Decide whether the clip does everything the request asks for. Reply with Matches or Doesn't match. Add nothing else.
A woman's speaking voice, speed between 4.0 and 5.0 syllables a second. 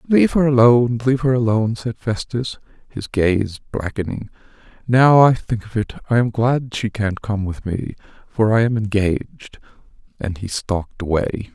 Doesn't match